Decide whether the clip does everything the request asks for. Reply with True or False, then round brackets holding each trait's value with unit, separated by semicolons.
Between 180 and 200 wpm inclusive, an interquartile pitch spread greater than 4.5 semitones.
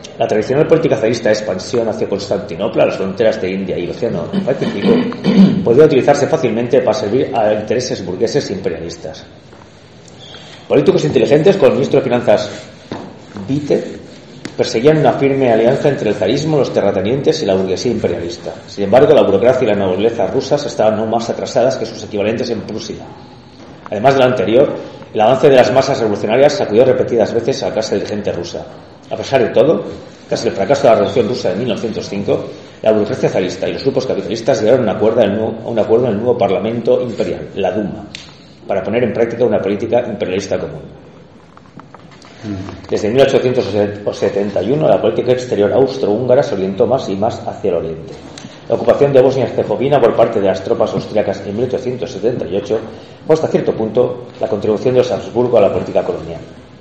False (170 wpm; 5.2 semitones)